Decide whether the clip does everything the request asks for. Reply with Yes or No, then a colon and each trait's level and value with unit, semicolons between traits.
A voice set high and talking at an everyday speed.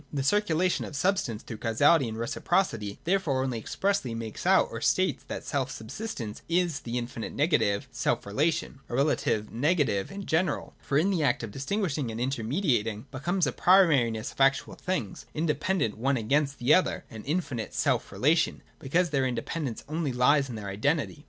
No: medium, 140 Hz; average, 180 wpm